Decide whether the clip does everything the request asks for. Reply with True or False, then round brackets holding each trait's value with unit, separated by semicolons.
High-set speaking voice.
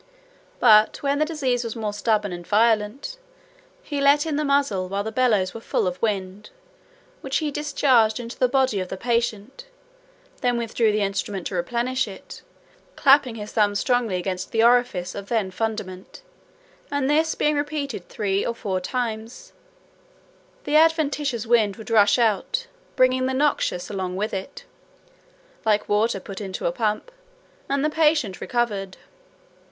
True (230 Hz)